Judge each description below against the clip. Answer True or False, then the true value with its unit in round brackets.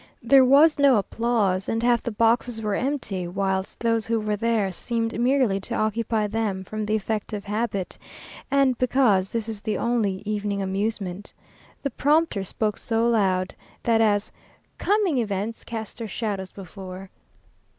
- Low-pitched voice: False (220 Hz)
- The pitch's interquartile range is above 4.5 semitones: False (3.0 semitones)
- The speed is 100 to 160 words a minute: True (155 wpm)